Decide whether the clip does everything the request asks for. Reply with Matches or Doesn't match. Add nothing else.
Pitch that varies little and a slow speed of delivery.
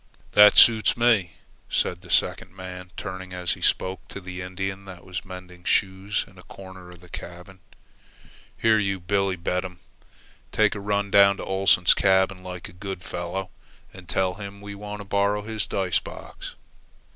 Doesn't match